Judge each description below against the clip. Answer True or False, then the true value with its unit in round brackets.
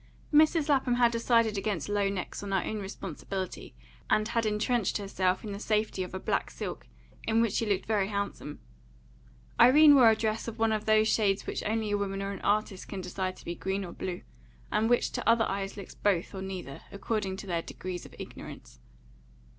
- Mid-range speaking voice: False (205 Hz)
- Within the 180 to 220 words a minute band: True (200 wpm)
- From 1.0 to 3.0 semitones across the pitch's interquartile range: True (2.6 semitones)